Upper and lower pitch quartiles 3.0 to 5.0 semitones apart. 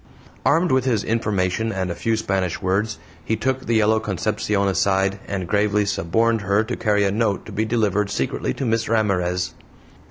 No: narrow, 2.5 semitones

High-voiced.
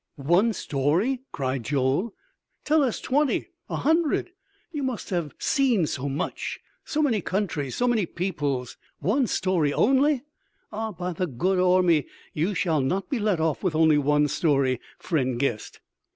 No: medium, 180 Hz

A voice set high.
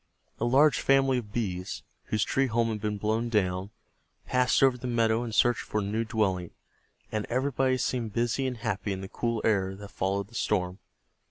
No: low, 110 Hz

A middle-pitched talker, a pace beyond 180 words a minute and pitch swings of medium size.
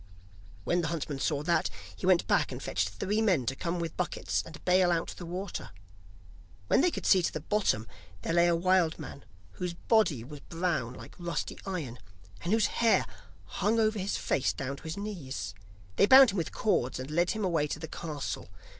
Yes: medium, 170 Hz; average, 200 wpm; average, 4.4 semitones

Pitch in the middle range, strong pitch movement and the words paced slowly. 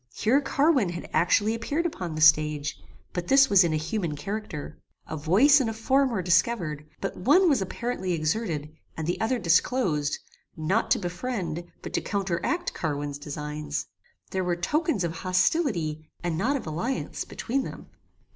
No: medium, 180 Hz; wide, 7.5 semitones; average, 165 wpm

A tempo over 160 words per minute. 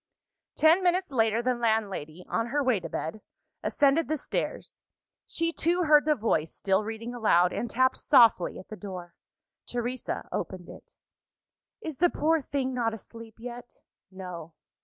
No: average, 155 wpm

